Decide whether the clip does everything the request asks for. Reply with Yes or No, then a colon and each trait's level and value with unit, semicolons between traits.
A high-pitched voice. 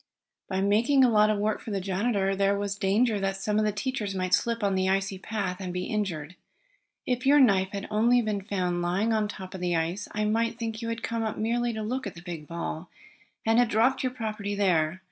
Yes: high, 205 Hz